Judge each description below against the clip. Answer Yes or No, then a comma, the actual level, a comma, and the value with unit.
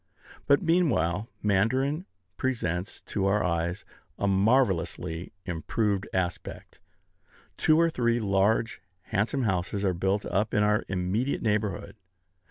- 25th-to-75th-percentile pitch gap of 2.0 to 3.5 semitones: No, average, 4.0 semitones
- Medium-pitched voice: No, low, 105 Hz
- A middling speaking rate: No, slow, 115 wpm